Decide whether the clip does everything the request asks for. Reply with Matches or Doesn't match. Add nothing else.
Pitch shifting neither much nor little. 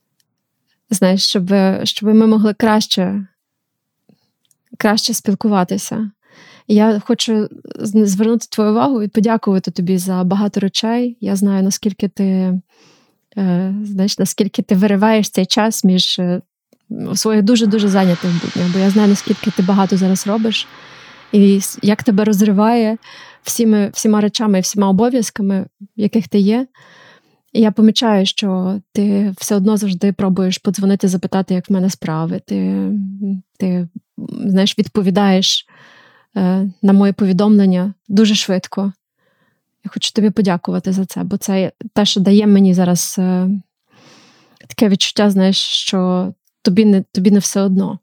Doesn't match